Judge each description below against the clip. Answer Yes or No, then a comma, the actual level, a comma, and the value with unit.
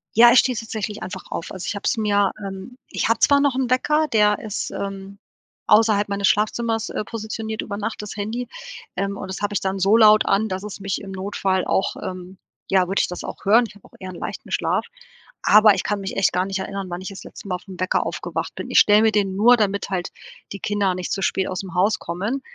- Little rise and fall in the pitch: Yes, narrow, 2.2 semitones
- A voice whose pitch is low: No, high, 200 Hz